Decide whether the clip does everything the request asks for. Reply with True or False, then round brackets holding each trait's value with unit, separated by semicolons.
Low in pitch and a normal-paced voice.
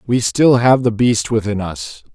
True (115 Hz; 195 wpm)